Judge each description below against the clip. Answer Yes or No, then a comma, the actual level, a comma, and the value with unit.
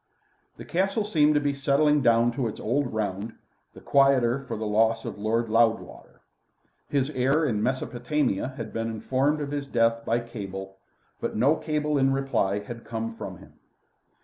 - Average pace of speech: Yes, average, 170 wpm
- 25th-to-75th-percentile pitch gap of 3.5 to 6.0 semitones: Yes, average, 4.0 semitones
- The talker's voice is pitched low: Yes, low, 120 Hz